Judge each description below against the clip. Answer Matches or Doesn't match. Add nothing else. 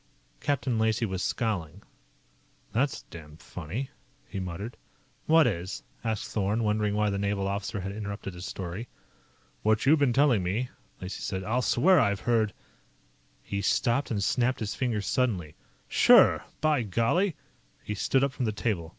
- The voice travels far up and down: Doesn't match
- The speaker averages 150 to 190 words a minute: Matches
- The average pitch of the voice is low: Matches